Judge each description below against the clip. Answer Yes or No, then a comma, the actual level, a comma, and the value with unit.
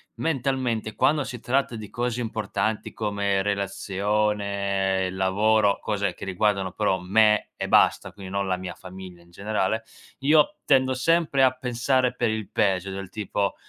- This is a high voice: No, low, 105 Hz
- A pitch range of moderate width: Yes, average, 3.8 semitones